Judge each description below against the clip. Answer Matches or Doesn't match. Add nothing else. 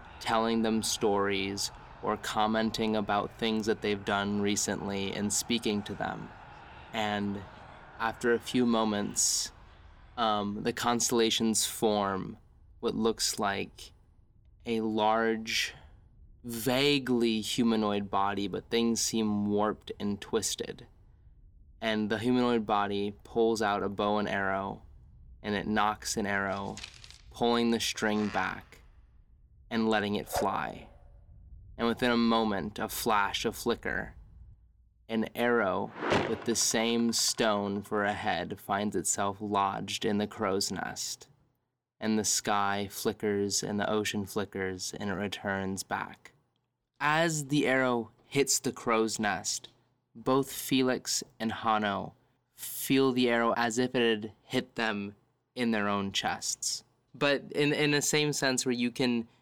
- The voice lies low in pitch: Matches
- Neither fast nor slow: Doesn't match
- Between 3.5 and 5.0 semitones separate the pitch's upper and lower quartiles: Doesn't match